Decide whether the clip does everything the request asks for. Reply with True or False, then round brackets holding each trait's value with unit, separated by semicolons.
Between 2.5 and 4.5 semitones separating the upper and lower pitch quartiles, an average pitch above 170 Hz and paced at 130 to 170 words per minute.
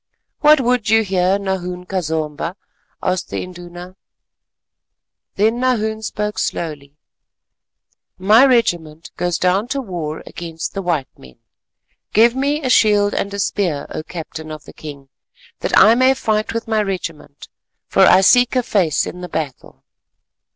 False (4.9 semitones; 190 Hz; 150 wpm)